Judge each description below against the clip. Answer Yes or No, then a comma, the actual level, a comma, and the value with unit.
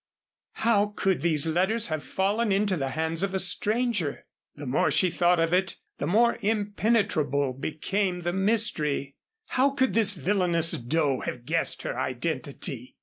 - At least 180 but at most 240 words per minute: No, average, 150 wpm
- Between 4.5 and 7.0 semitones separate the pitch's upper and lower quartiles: Yes, wide, 5.5 semitones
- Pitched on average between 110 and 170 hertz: No, medium, 180 Hz